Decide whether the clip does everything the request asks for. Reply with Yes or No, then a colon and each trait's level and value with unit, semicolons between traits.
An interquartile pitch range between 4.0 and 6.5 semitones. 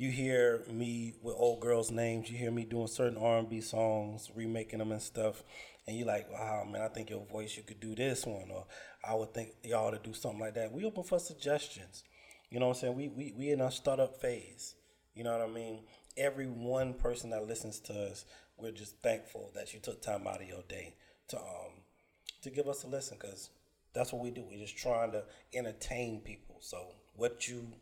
No: narrow, 2.4 semitones